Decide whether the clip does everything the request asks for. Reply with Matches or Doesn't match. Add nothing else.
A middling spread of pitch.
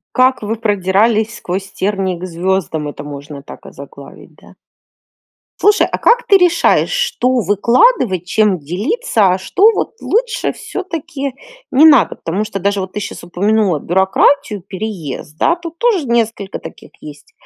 Doesn't match